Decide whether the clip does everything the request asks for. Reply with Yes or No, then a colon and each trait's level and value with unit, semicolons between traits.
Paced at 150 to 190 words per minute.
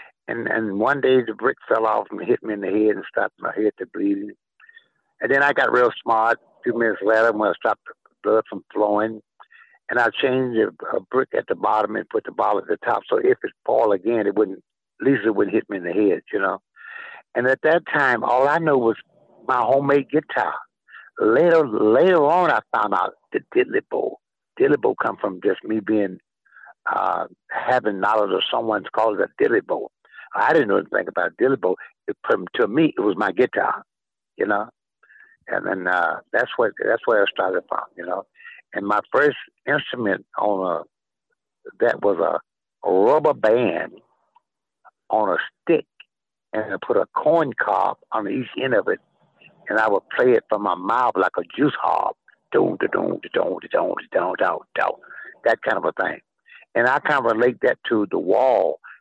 No: average, 200 wpm